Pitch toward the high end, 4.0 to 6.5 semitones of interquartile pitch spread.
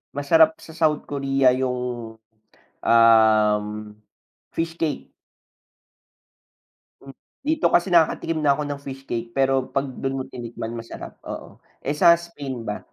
No: low, 135 Hz; average, 4.6 semitones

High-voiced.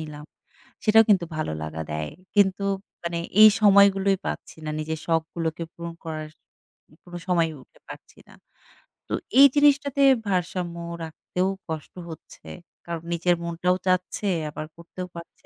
No: medium, 170 Hz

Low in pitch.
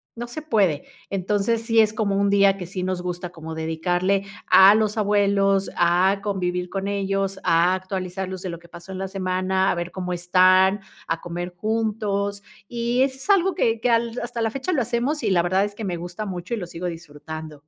No: high, 195 Hz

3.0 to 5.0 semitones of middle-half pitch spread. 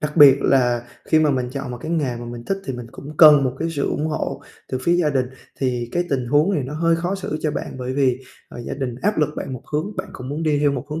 Yes: average, 3.6 semitones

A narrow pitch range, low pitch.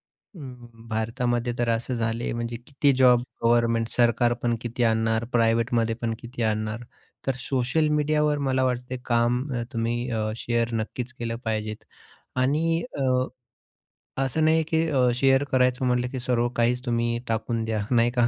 Yes: narrow, 1.8 semitones; low, 120 Hz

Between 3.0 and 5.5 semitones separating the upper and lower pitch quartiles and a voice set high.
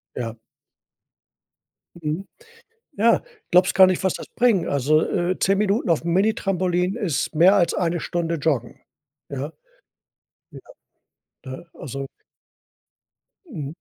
No: average, 4.1 semitones; medium, 175 Hz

